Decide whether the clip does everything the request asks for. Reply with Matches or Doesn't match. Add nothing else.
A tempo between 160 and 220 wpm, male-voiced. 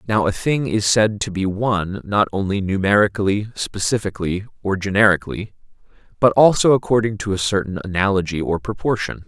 Doesn't match